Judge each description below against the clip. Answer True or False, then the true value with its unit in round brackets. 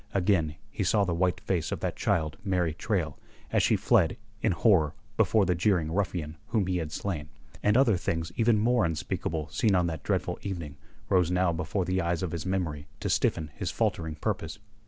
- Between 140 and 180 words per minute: False (195 wpm)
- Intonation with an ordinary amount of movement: True (3.4 semitones)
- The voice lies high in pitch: False (90 Hz)